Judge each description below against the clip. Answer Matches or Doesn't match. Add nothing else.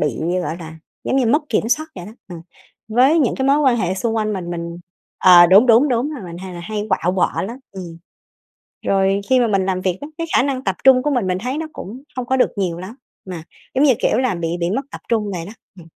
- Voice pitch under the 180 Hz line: Doesn't match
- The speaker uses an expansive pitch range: Matches